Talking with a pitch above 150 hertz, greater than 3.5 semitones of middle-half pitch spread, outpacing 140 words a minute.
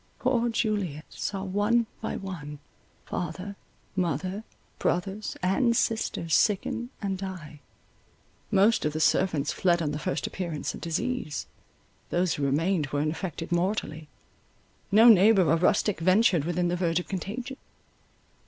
No: medium, 185 Hz; average, 4.0 semitones; slow, 135 wpm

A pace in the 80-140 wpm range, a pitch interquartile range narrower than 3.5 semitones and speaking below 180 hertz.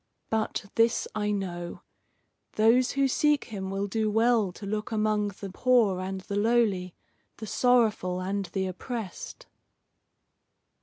No: slow, 135 wpm; average, 3.1 semitones; high, 210 Hz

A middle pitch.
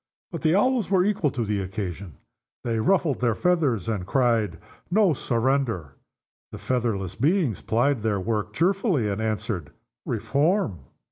No: low, 120 Hz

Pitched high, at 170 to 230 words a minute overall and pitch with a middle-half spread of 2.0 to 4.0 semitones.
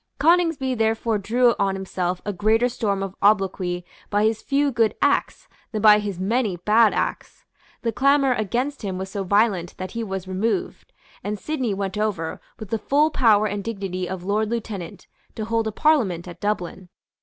Yes: high, 210 Hz; average, 180 wpm; average, 3.4 semitones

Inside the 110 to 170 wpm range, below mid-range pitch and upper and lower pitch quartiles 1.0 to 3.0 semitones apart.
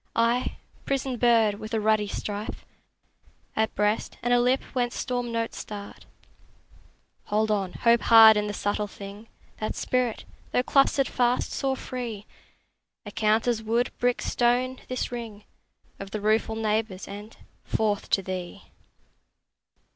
No: average, 140 wpm; high, 220 Hz; narrow, 2.6 semitones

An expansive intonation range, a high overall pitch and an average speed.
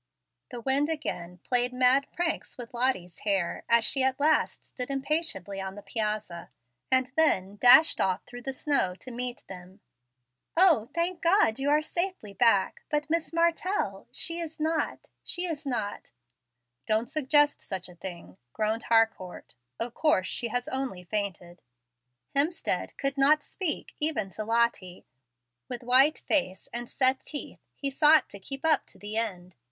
Yes: wide, 6.9 semitones; high, 245 Hz; average, 160 wpm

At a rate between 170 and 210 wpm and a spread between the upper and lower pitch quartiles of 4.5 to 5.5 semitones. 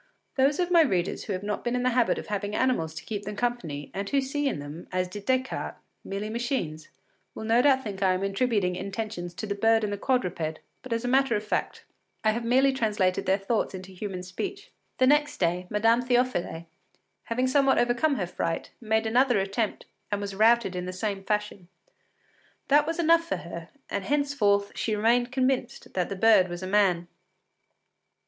Yes: average, 195 wpm; average, 4.9 semitones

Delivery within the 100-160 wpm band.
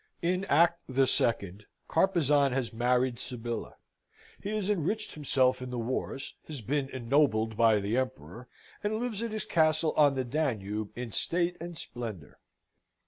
Yes: average, 150 wpm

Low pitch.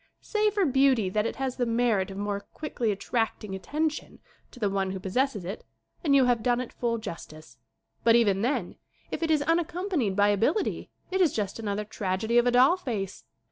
No: high, 235 Hz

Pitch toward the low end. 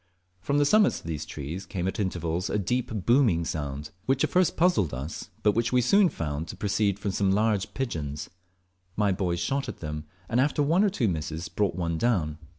Yes: low, 100 Hz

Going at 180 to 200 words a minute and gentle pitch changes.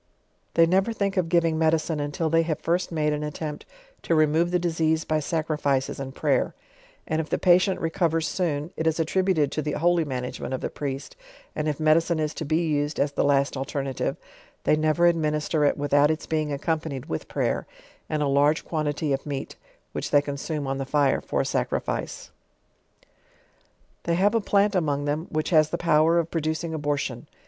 Yes: average, 190 wpm; narrow, 2.3 semitones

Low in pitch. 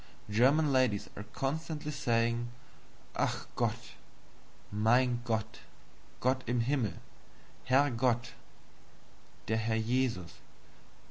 Yes: low, 120 Hz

